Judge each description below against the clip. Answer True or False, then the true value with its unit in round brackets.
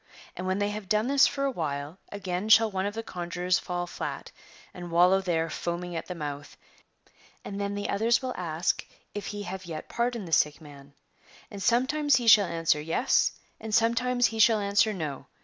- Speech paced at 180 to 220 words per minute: True (200 wpm)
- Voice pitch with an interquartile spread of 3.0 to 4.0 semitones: False (4.5 semitones)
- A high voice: True (195 Hz)